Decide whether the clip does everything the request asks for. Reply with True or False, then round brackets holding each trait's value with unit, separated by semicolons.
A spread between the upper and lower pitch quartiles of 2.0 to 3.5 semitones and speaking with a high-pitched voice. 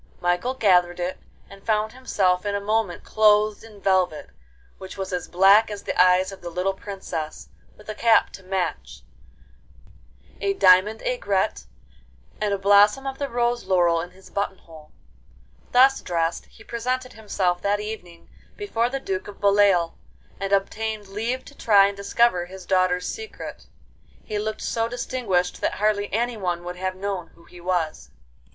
True (3.2 semitones; 200 Hz)